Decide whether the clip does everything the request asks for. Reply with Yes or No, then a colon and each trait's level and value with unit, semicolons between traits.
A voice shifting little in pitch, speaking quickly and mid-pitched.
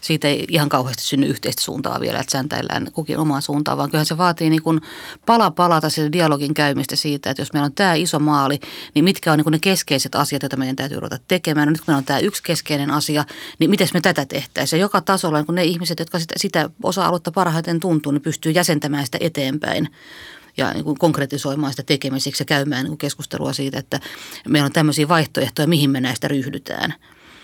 No: average, 3.0 semitones; fast, 205 wpm; medium, 150 Hz